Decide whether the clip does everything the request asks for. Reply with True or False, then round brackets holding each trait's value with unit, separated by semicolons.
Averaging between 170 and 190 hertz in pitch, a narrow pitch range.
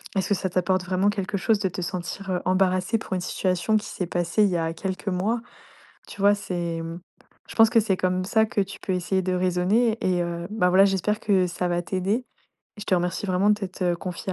True (185 Hz; 2.1 semitones)